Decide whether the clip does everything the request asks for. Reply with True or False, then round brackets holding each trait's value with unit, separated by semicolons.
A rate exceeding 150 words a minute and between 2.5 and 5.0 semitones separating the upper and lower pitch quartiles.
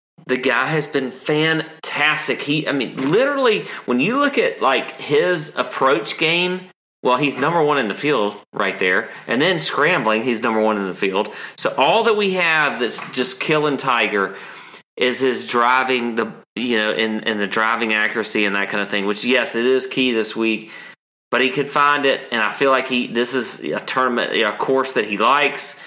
False (200 wpm; 5.4 semitones)